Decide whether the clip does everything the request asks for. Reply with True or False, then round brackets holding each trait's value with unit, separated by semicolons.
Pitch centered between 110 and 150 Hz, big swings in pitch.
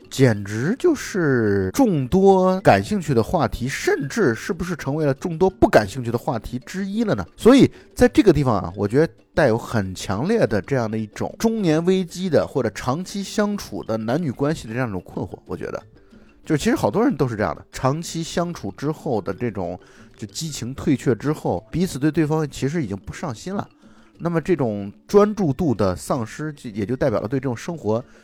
True (140 Hz; 8.3 semitones)